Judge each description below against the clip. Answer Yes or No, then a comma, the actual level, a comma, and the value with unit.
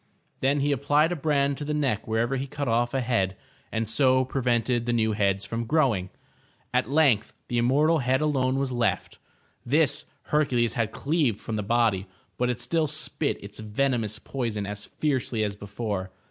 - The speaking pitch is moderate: No, low, 120 Hz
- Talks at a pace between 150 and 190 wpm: Yes, average, 180 wpm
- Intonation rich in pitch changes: No, average, 4.2 semitones